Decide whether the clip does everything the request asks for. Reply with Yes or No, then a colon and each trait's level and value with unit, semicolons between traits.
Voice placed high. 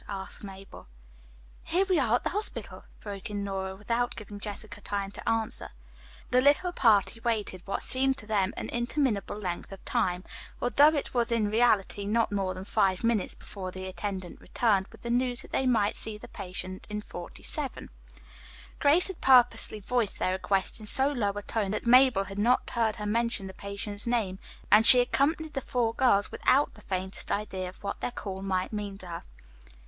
Yes: high, 210 Hz